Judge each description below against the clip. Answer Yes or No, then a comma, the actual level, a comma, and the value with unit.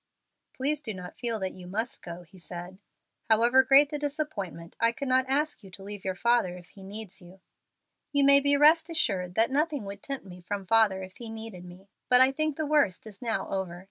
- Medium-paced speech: No, fast, 215 wpm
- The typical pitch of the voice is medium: No, high, 220 Hz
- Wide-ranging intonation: Yes, wide, 6.5 semitones